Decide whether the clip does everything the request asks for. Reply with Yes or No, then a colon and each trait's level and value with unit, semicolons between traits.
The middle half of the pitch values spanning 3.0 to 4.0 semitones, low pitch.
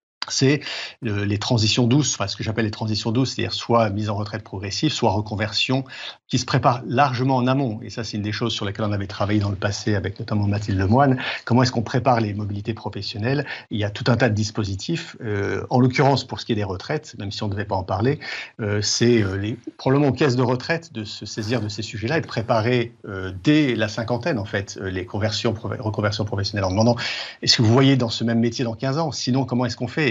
Yes: average, 3.5 semitones; low, 115 Hz